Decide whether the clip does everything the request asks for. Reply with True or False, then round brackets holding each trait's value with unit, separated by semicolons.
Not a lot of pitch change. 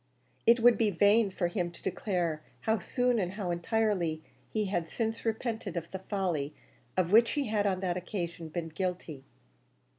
False (4.3 semitones)